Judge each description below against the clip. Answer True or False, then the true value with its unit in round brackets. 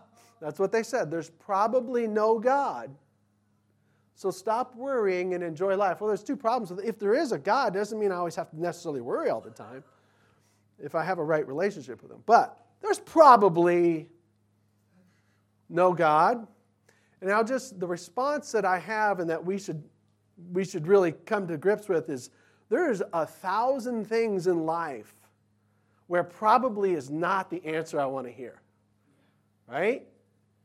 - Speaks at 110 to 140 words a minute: False (170 wpm)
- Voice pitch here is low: False (175 Hz)